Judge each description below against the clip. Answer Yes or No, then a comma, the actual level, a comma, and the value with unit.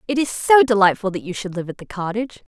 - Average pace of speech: No, fast, 260 wpm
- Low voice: No, high, 215 Hz